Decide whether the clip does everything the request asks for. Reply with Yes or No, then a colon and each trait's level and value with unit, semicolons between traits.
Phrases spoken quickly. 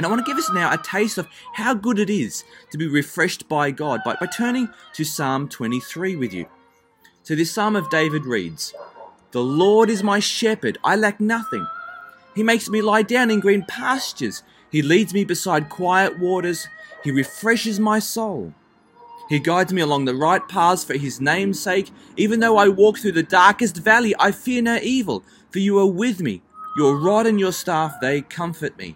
No: average, 195 wpm